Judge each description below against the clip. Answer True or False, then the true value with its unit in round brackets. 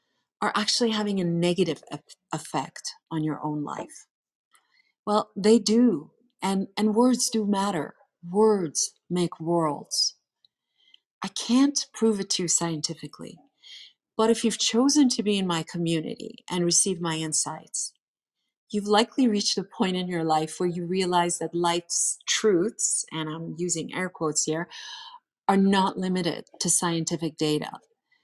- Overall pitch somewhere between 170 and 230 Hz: True (185 Hz)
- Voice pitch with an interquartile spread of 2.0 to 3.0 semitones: False (5.1 semitones)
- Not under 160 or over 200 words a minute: False (145 wpm)